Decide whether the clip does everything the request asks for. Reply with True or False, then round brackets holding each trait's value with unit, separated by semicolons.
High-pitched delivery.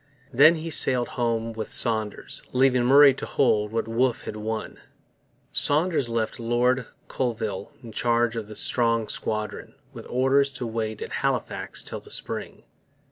False (120 Hz)